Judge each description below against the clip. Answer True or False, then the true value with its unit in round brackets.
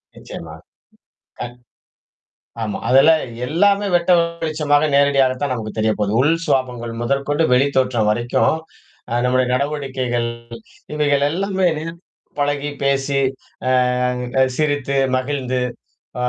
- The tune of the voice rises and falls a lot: False (2.9 semitones)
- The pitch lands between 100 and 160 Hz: True (140 Hz)